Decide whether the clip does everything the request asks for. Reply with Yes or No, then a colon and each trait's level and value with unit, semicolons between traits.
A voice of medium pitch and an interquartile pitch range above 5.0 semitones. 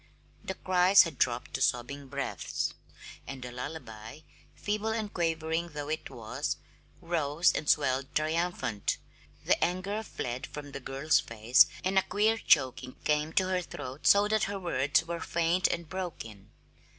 Yes: medium, 155 Hz; wide, 5.4 semitones